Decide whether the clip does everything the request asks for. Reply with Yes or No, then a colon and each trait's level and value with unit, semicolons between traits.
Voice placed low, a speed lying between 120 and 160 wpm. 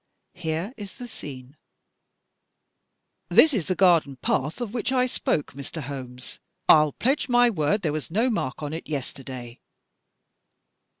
No: medium, 160 Hz; average, 145 wpm